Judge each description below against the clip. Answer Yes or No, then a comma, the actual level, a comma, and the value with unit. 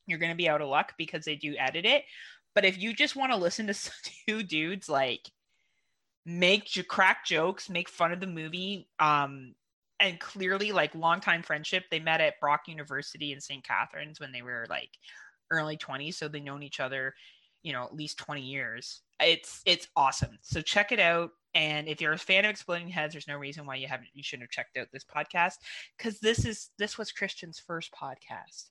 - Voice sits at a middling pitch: Yes, medium, 160 Hz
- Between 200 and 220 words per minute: Yes, fast, 205 wpm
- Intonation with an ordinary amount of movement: Yes, average, 4.3 semitones